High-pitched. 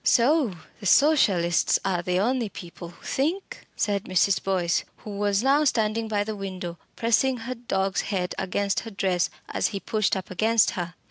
Yes: high, 200 Hz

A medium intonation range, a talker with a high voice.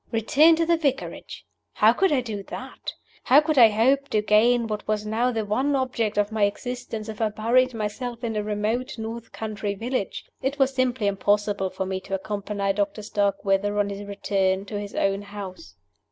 Yes: average, 3.4 semitones; high, 215 Hz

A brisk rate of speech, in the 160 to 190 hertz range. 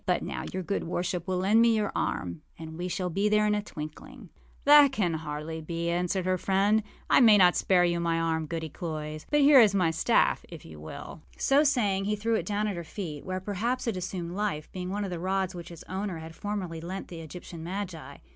Yes: fast, 230 wpm; medium, 185 Hz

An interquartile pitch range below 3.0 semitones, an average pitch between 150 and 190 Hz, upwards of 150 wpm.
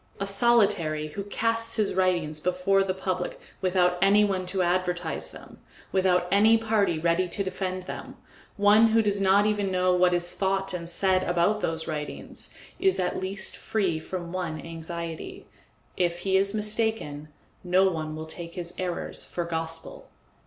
Yes: narrow, 2.5 semitones; medium, 185 Hz; average, 160 wpm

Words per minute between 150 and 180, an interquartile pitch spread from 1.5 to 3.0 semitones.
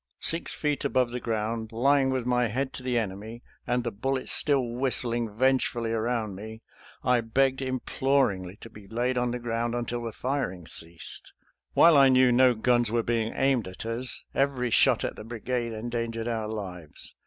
Yes: average, 175 wpm; narrow, 2.5 semitones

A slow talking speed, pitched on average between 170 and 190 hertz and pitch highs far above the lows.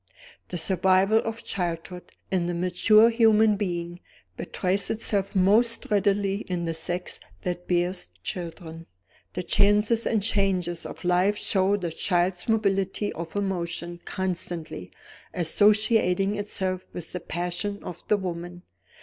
No: slow, 125 wpm; medium, 185 Hz; average, 2.7 semitones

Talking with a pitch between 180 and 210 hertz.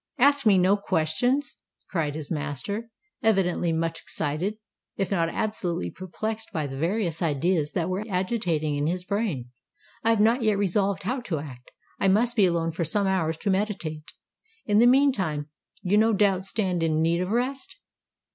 Yes: medium, 185 Hz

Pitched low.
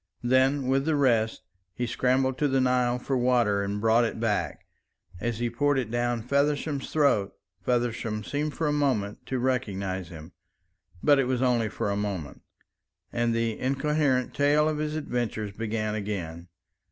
Yes: low, 120 Hz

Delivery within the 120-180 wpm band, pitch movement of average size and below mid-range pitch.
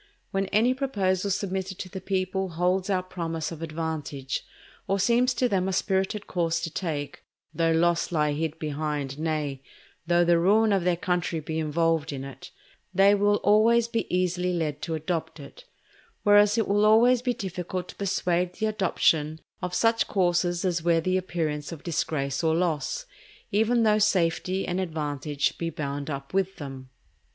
No: average, 170 wpm; average, 3.6 semitones; medium, 180 Hz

